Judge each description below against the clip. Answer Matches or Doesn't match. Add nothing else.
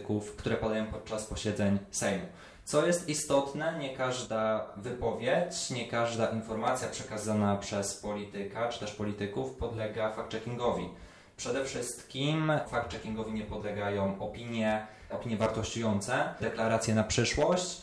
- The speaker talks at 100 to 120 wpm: Matches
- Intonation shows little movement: Matches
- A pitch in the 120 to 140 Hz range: Doesn't match